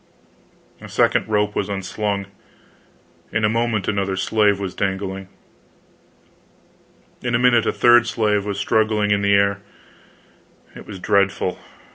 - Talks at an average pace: No, slow, 130 wpm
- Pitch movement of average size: No, narrow, 1.8 semitones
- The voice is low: Yes, low, 105 Hz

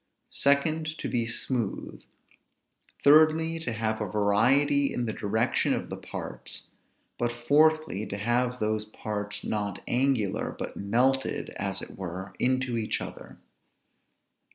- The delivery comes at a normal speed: No, slow, 130 wpm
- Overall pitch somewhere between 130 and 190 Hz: No, low, 120 Hz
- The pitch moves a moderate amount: Yes, average, 4.8 semitones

